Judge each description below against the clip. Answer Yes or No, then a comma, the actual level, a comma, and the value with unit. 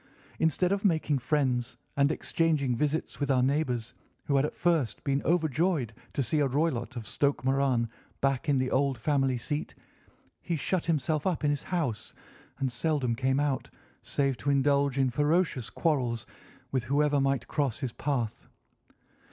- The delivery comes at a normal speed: Yes, average, 160 wpm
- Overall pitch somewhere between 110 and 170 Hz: Yes, medium, 140 Hz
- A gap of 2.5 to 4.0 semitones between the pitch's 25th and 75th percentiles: Yes, average, 2.9 semitones